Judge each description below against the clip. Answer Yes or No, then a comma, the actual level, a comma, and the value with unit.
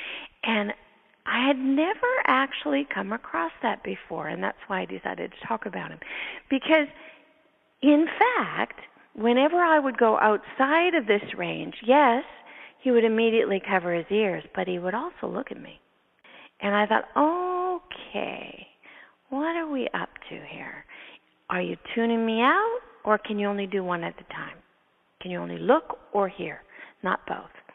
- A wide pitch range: Yes, wide, 7.0 semitones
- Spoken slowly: No, average, 160 wpm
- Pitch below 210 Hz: No, very high, 265 Hz